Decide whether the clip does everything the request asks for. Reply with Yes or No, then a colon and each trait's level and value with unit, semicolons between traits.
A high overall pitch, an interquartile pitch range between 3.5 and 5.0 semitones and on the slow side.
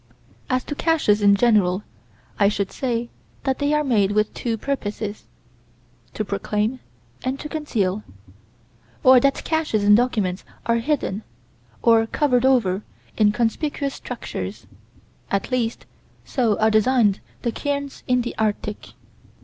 Yes: high, 230 Hz; average, 4.2 semitones; slow, 130 wpm